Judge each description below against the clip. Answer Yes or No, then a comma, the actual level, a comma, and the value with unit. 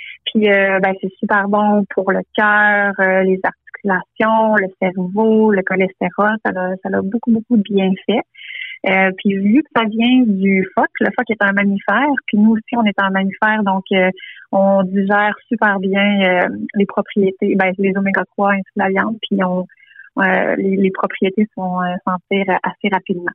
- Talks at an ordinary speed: Yes, average, 190 wpm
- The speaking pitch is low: No, high, 200 Hz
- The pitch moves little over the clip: Yes, narrow, 2.2 semitones